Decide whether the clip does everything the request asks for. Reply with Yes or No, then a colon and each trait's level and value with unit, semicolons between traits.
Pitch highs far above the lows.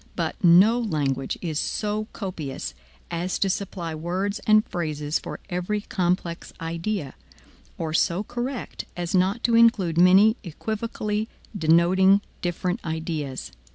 No: average, 4.2 semitones